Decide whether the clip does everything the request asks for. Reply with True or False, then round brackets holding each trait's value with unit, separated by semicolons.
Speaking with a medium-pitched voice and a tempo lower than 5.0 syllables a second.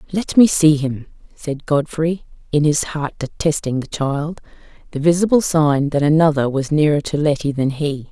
True (150 Hz; 4.7 syllables/s)